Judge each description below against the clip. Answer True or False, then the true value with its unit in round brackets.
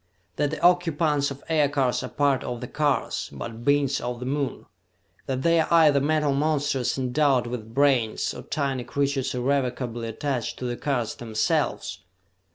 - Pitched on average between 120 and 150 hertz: True (140 Hz)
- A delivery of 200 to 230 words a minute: False (160 wpm)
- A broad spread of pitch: False (2.9 semitones)